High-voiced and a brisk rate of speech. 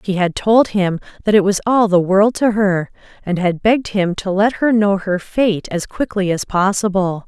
Yes: high, 195 Hz; fast, 215 wpm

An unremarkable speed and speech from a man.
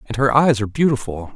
No: fast, 220 wpm; male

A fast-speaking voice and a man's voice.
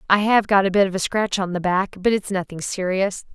No: fast, 270 wpm; female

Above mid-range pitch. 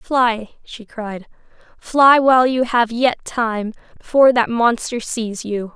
Yes: high, 240 Hz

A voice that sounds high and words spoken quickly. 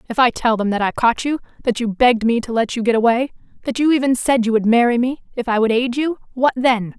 Yes: high, 240 Hz; fast, 265 wpm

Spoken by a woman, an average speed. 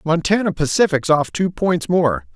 No: male; average, 155 wpm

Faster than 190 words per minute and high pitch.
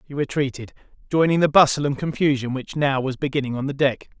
No: average, 200 wpm; medium, 140 Hz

